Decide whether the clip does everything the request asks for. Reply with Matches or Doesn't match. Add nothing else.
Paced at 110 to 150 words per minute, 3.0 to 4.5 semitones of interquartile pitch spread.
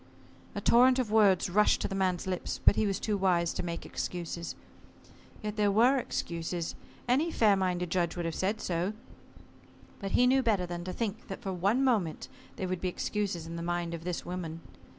Doesn't match